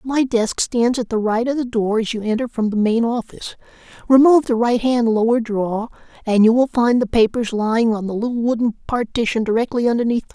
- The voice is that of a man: Yes, male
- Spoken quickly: Yes, fast, 215 wpm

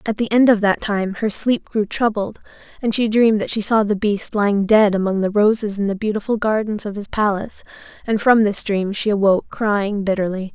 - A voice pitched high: Yes, high, 210 Hz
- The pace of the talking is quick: Yes, fast, 215 wpm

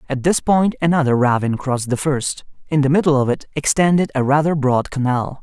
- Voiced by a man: Yes, male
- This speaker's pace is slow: No, average, 200 wpm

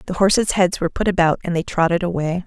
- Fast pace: Yes, fast, 245 wpm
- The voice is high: No, medium, 175 Hz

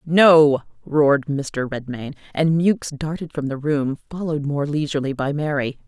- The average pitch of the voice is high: No, medium, 150 Hz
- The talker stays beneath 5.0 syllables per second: Yes, 4.7 syllables/s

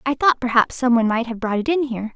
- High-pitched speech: Yes, high, 245 Hz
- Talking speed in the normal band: No, fast, 305 wpm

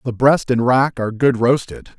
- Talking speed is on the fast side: Yes, fast, 210 wpm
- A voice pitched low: Yes, low, 125 Hz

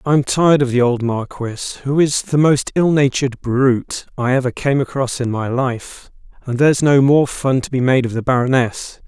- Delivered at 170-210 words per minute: Yes, average, 200 wpm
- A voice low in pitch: Yes, low, 130 Hz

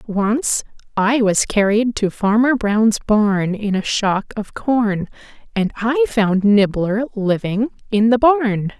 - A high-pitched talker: Yes, high, 220 Hz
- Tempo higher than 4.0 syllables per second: No, 3.4 syllables/s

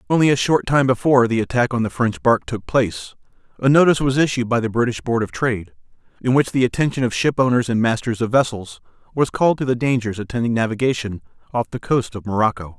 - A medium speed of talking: No, fast, 215 wpm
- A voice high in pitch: No, low, 120 Hz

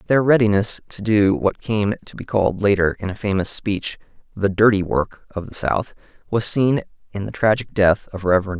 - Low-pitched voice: Yes, low, 100 Hz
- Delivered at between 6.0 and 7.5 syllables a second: No, 4.9 syllables/s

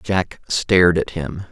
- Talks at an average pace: Yes, average, 160 wpm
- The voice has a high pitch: No, very low, 85 Hz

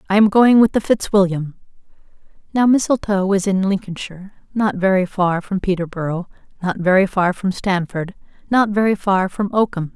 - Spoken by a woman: Yes, female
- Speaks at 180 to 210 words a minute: No, average, 155 wpm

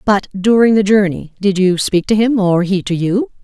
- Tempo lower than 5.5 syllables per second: Yes, 4.8 syllables/s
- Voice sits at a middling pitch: No, high, 200 Hz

